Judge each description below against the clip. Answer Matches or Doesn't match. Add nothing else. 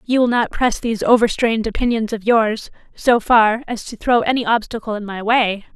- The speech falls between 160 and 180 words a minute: Doesn't match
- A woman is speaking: Matches